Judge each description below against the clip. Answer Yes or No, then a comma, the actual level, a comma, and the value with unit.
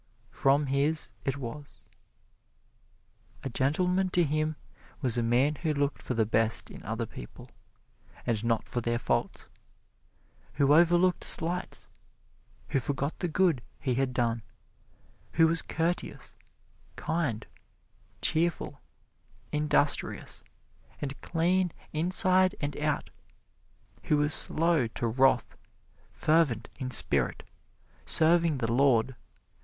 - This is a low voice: No, medium, 145 Hz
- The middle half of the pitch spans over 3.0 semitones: Yes, average, 4.6 semitones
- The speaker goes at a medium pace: No, slow, 115 wpm